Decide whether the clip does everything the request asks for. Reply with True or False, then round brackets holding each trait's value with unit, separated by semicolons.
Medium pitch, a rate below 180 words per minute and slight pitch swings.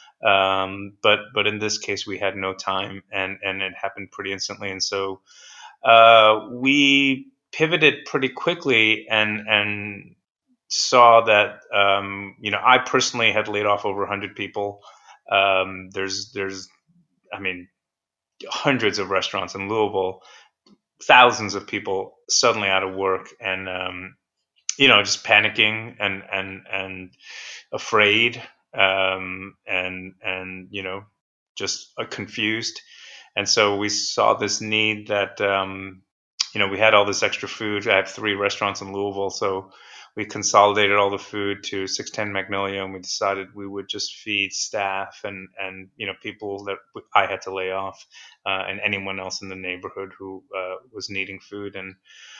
False (100 Hz; 155 wpm; 1.6 semitones)